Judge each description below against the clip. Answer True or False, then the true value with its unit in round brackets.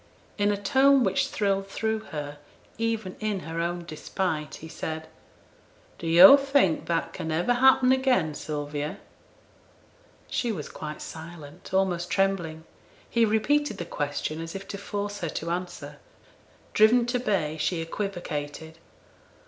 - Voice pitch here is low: False (180 Hz)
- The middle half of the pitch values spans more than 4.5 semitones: True (5.2 semitones)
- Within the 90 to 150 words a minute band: True (140 wpm)